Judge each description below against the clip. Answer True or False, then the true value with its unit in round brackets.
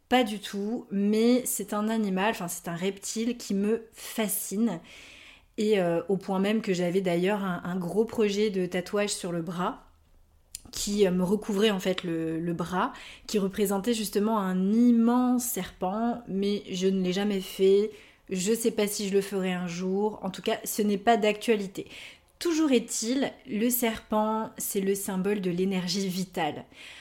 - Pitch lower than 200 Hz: False (205 Hz)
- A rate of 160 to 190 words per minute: True (175 wpm)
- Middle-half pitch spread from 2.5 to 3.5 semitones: True (3.0 semitones)